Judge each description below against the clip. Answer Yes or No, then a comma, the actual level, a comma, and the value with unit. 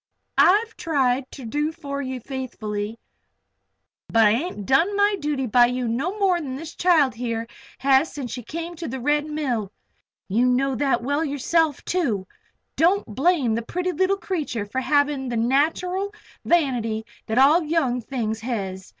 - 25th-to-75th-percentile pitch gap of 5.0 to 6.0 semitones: Yes, wide, 5.4 semitones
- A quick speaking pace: No, average, 165 wpm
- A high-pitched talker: Yes, very high, 270 Hz